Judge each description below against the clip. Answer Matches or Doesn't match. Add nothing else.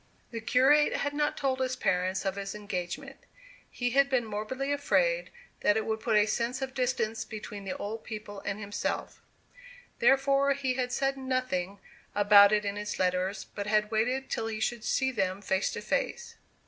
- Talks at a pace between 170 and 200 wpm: Matches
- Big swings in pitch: Doesn't match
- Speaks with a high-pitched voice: Matches